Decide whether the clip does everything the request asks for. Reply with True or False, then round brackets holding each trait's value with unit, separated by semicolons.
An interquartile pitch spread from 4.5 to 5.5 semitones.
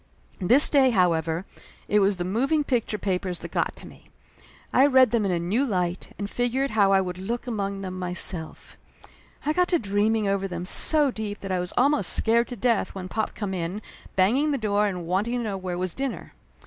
True (4.8 semitones)